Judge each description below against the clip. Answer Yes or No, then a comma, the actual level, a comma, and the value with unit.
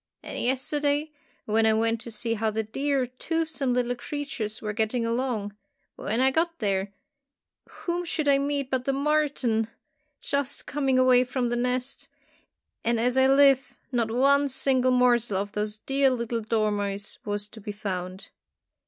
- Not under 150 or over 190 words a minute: Yes, average, 160 wpm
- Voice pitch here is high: Yes, very high, 250 Hz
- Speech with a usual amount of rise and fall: Yes, average, 3.9 semitones